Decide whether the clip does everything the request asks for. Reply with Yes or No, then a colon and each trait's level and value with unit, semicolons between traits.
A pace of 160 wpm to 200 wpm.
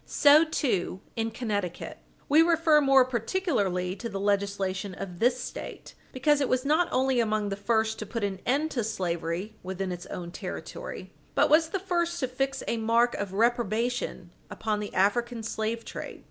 Yes: average, 175 wpm